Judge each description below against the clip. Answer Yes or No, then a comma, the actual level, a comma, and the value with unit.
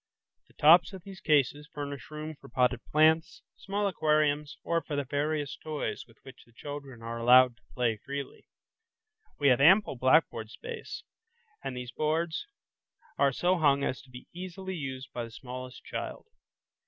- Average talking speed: Yes, average, 165 wpm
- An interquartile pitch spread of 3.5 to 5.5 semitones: Yes, average, 3.8 semitones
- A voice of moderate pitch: Yes, medium, 145 Hz